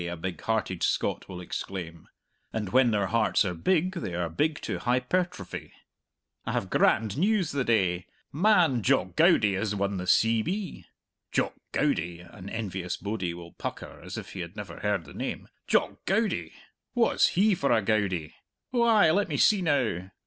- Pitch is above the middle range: No, low, 110 Hz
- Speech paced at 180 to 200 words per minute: No, average, 170 wpm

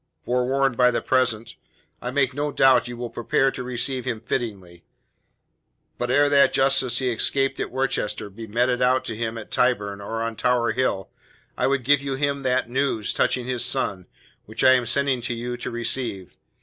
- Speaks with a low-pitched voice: Yes, low, 125 Hz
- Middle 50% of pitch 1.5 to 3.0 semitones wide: Yes, narrow, 2.4 semitones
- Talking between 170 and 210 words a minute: Yes, average, 195 wpm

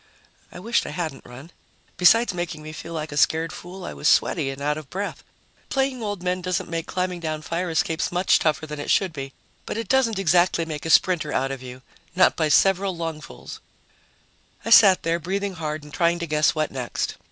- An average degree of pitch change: Yes, average, 3.2 semitones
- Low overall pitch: No, medium, 165 Hz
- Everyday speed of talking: No, fast, 210 wpm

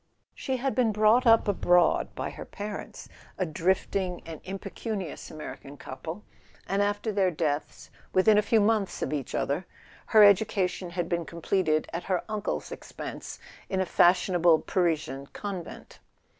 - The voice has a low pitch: No, medium, 185 Hz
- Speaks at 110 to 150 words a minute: Yes, average, 145 wpm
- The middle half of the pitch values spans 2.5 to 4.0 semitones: Yes, average, 3.7 semitones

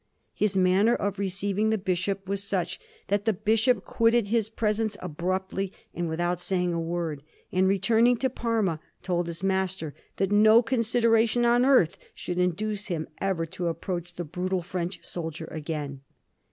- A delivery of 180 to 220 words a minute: No, average, 155 wpm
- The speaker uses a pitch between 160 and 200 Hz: Yes, high, 190 Hz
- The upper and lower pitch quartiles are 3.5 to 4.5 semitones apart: Yes, average, 3.8 semitones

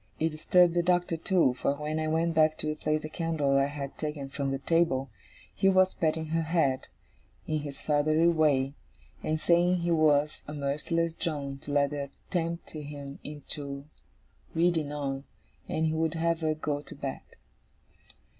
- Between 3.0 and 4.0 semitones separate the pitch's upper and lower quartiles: No, narrow, 2.5 semitones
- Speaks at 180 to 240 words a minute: No, average, 170 wpm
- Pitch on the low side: No, medium, 155 Hz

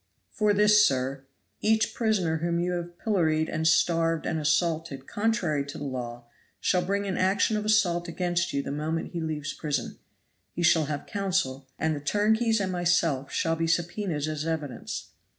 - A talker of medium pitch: Yes, medium, 165 Hz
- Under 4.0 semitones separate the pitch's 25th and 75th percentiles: No, average, 4.3 semitones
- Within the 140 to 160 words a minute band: No, average, 170 wpm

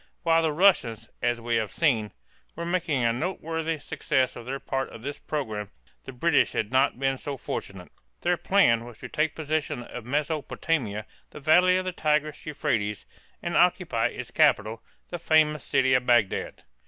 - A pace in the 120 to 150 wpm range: No, average, 170 wpm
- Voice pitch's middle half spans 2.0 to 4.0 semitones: No, average, 5.2 semitones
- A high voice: No, medium, 140 Hz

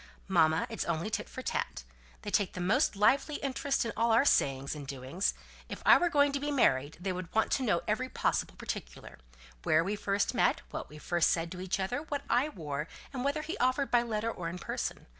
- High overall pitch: Yes, high, 205 Hz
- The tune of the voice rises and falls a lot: Yes, wide, 7.6 semitones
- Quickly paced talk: Yes, fast, 220 wpm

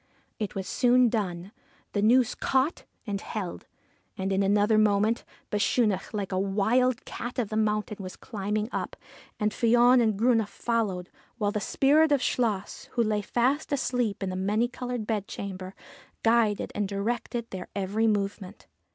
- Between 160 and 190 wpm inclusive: No, average, 150 wpm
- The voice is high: Yes, high, 215 Hz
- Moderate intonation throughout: Yes, average, 3.2 semitones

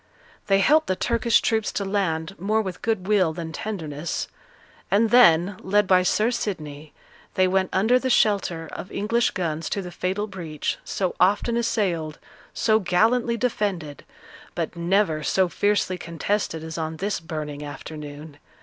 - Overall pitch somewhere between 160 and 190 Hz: Yes, medium, 185 Hz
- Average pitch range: Yes, average, 4.5 semitones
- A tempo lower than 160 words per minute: Yes, average, 150 wpm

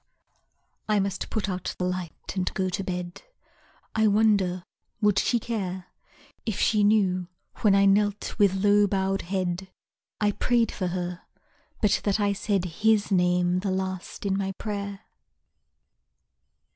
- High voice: Yes, high, 195 Hz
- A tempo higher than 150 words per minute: No, average, 145 wpm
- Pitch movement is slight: Yes, narrow, 2.1 semitones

